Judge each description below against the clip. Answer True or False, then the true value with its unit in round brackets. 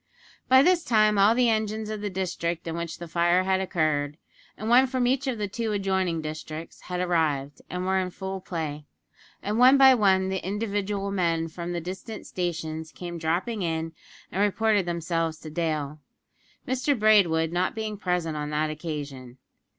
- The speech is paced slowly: False (175 wpm)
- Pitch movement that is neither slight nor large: True (4.5 semitones)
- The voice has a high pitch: False (180 Hz)